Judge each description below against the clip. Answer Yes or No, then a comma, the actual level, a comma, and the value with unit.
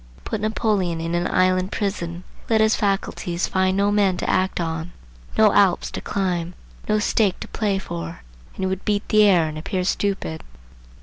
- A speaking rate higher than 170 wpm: Yes, average, 180 wpm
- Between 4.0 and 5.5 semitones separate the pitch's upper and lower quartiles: No, average, 2.9 semitones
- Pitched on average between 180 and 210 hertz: Yes, high, 190 Hz